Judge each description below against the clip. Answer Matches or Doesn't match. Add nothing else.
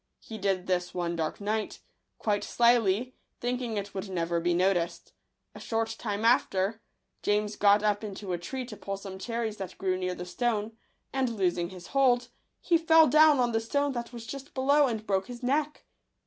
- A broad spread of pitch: Doesn't match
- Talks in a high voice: Matches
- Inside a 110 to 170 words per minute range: Doesn't match